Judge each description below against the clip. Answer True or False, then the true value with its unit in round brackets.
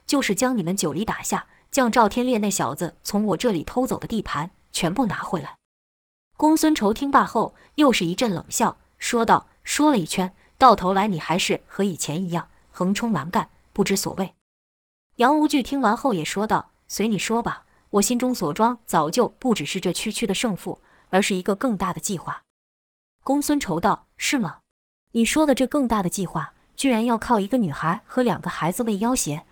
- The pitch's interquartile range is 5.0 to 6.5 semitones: True (5.5 semitones)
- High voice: True (205 Hz)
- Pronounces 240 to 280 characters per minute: True (275 characters per minute)